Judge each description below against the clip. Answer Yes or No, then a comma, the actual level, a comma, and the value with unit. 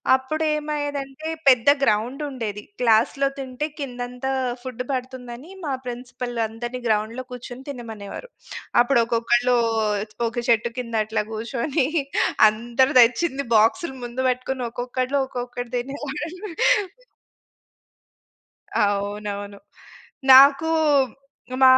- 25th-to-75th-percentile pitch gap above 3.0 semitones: No, narrow, 2.5 semitones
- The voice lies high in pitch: Yes, very high, 250 Hz